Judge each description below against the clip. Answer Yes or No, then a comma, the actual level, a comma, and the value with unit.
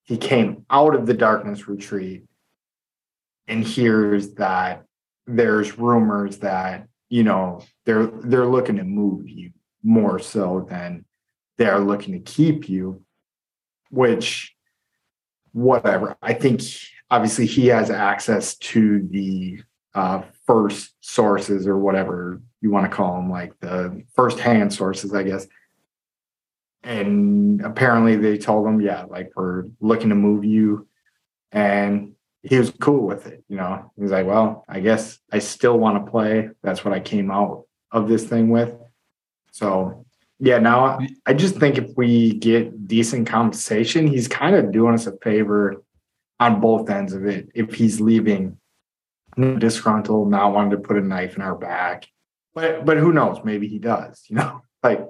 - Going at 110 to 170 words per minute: Yes, average, 155 wpm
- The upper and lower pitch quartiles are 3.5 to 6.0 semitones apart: No, average, 3.0 semitones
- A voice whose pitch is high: No, low, 110 Hz